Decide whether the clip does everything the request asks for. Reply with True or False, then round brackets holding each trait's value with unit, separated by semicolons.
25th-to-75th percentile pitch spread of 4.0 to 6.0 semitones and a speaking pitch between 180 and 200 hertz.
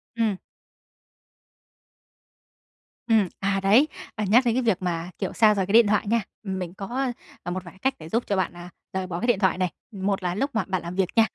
False (3.5 semitones; 195 Hz)